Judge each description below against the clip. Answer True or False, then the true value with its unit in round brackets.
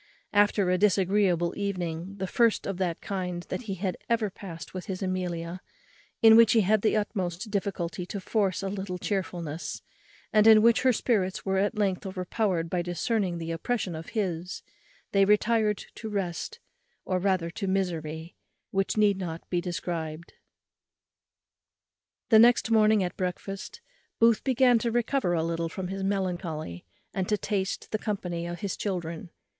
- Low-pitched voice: False (190 Hz)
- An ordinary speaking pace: True (160 wpm)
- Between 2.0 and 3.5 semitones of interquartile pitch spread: True (3.2 semitones)